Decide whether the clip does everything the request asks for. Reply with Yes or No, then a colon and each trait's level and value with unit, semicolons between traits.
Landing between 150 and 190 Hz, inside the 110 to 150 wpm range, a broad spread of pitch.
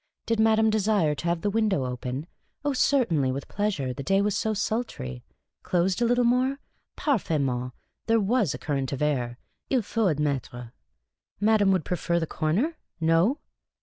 No: medium, 185 Hz; average, 160 wpm; wide, 7.8 semitones